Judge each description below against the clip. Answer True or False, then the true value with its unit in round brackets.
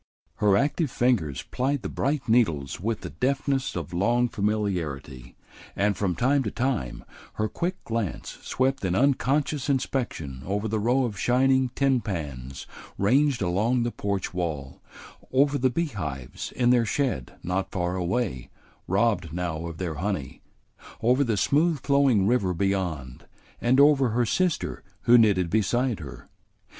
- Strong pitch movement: True (6.7 semitones)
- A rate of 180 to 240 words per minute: False (145 wpm)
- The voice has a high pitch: False (110 Hz)